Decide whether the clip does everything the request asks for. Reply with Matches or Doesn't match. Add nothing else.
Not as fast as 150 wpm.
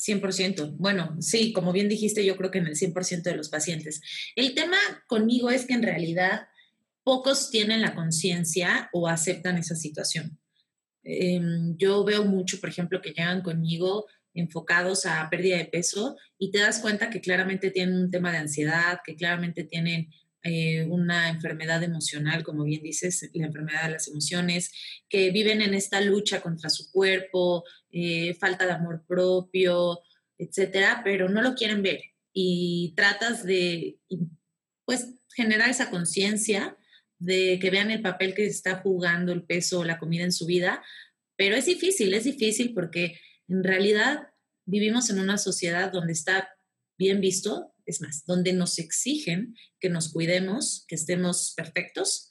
Doesn't match